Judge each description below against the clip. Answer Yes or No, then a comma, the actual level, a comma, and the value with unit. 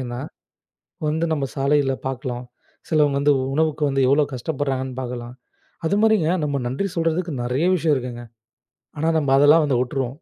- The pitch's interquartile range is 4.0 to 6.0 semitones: No, average, 3.4 semitones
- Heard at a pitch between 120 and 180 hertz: Yes, medium, 140 Hz